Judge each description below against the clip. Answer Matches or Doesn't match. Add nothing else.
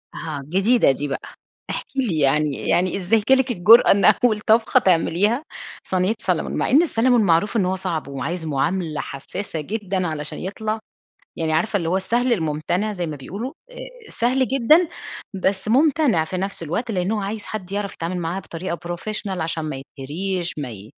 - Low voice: Doesn't match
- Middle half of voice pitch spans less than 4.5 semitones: Doesn't match